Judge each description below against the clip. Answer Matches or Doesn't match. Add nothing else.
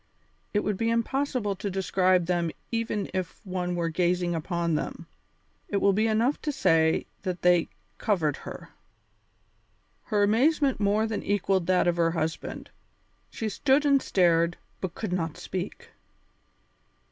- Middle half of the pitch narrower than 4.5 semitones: Matches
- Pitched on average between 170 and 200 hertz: Matches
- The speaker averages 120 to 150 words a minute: Matches